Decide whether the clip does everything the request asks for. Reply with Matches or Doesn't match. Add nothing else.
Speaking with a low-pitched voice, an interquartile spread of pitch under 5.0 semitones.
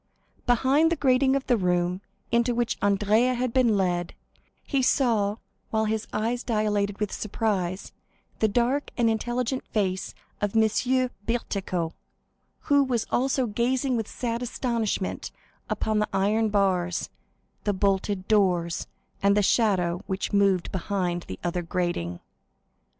Doesn't match